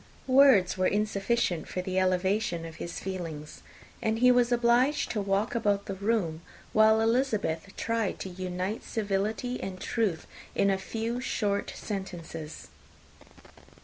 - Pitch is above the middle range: Yes, high, 200 Hz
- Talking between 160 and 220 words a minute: No, slow, 135 wpm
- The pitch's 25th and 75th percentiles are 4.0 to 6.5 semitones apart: No, average, 3.6 semitones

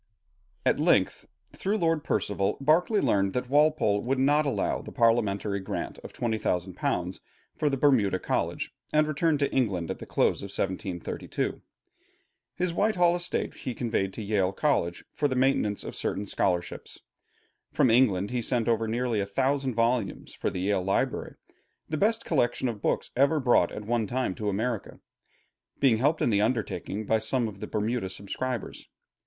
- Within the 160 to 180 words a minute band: Yes, average, 165 wpm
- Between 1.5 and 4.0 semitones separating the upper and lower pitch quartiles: No, wide, 5.5 semitones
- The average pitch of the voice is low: Yes, low, 120 Hz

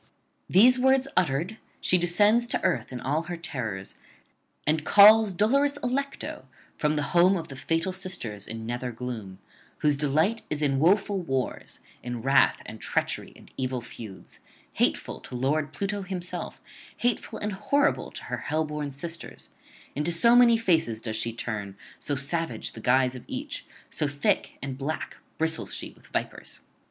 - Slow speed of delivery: No, average, 165 wpm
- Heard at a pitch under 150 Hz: No, medium, 155 Hz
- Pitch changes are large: Yes, wide, 7.1 semitones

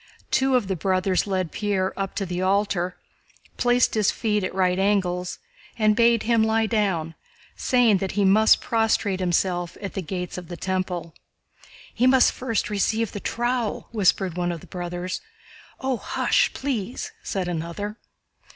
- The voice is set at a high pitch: Yes, high, 195 Hz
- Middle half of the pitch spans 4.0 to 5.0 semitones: No, average, 3.5 semitones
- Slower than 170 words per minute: Yes, average, 160 wpm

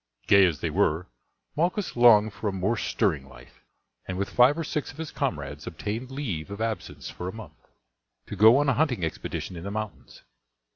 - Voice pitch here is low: Yes, low, 110 Hz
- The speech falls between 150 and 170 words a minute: No, average, 195 wpm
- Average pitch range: No, wide, 6.5 semitones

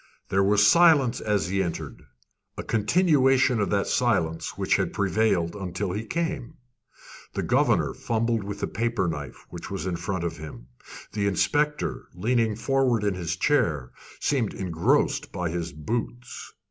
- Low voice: Yes, low, 105 Hz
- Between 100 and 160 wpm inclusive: Yes, average, 150 wpm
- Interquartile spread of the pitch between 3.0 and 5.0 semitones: No, wide, 5.5 semitones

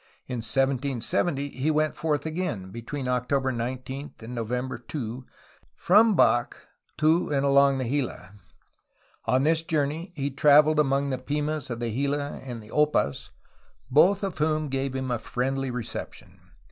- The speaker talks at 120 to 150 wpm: Yes, average, 145 wpm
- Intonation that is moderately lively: Yes, average, 3.1 semitones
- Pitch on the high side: No, low, 135 Hz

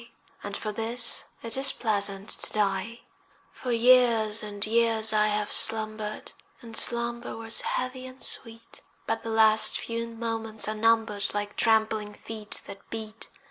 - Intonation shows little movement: Yes, narrow, 1.5 semitones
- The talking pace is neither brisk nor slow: Yes, average, 145 wpm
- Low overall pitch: No, high, 225 Hz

